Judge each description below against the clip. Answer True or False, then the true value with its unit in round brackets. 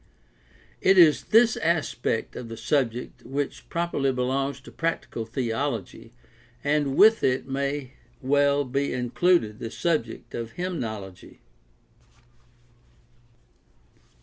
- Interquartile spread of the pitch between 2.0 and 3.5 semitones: False (4.1 semitones)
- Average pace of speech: False (105 wpm)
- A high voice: False (135 Hz)